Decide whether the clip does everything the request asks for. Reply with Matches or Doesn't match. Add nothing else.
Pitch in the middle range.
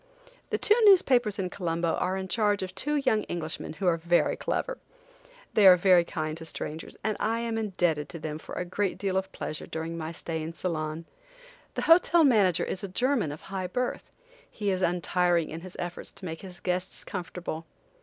Matches